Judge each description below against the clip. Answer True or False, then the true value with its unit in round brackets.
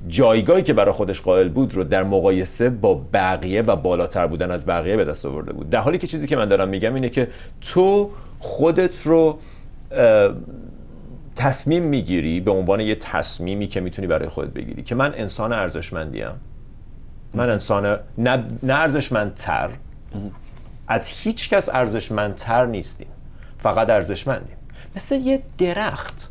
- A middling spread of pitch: False (8.1 semitones)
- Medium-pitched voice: False (115 Hz)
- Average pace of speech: True (140 wpm)